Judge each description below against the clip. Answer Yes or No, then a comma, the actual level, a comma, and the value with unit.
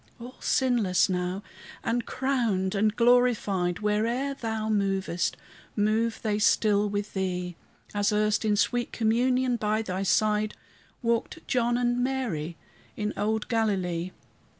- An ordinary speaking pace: No, slow, 125 wpm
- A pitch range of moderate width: Yes, average, 3.3 semitones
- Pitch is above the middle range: Yes, high, 215 Hz